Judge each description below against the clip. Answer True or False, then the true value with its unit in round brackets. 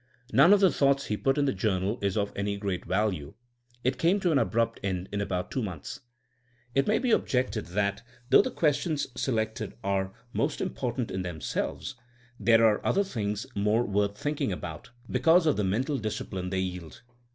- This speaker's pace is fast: False (185 wpm)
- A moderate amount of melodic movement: False (6.1 semitones)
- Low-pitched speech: True (110 Hz)